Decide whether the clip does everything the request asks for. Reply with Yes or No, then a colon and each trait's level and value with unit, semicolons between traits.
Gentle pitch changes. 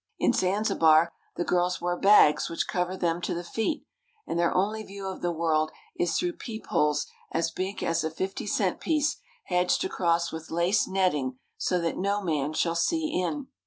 No: average, 3.1 semitones